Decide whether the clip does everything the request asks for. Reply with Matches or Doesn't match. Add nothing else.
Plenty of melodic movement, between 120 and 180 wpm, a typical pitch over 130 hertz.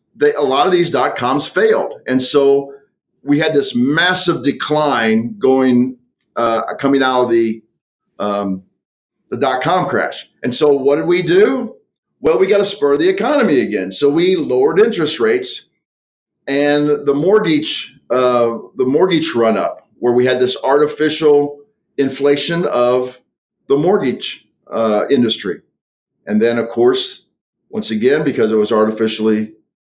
Matches